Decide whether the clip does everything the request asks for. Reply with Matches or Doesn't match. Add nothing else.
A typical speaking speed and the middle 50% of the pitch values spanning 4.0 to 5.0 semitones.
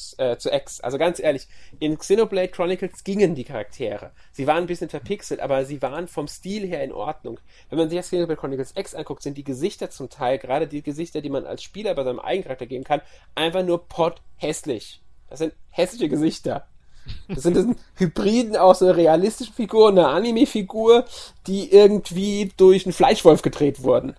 Matches